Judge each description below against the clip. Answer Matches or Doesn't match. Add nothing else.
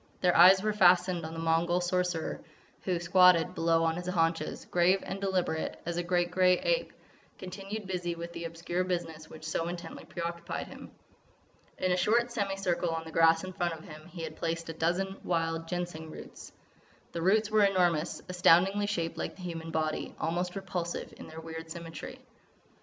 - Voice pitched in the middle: Matches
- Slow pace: Doesn't match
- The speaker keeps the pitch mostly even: Matches